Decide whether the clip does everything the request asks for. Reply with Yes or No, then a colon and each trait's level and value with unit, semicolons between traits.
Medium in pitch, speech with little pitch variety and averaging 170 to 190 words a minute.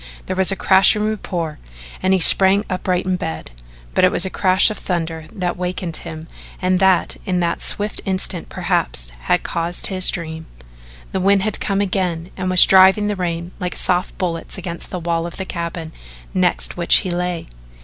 Yes: medium, 180 Hz; narrow, 2.0 semitones; average, 185 wpm